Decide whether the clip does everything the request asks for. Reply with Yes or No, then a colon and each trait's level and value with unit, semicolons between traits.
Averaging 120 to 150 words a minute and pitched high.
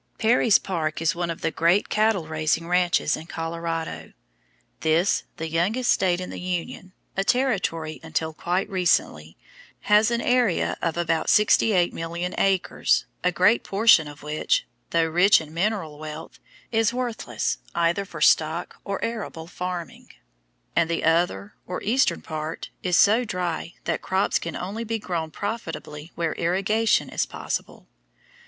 No: average, 145 wpm; medium, 175 Hz